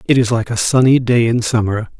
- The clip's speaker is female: No, male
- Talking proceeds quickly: Yes, fast, 240 wpm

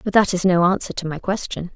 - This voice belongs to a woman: Yes, female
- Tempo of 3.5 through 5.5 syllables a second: No, 6.1 syllables/s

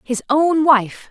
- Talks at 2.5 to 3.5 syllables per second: Yes, 3.2 syllables/s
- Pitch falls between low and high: No, very high, 275 Hz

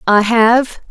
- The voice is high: Yes, high, 230 Hz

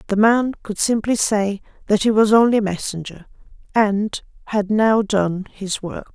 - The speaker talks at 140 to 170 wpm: Yes, average, 165 wpm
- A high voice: Yes, high, 210 Hz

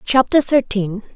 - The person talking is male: No, female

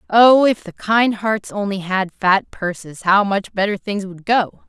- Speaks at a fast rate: No, average, 190 wpm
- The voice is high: Yes, high, 200 Hz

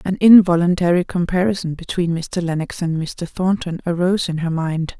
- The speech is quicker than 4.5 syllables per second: Yes, 5.2 syllables/s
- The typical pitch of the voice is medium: Yes, medium, 175 Hz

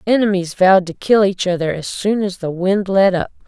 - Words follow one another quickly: Yes, fast, 225 wpm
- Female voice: Yes, female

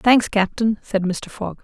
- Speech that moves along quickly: No, average, 185 wpm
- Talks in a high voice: Yes, high, 210 Hz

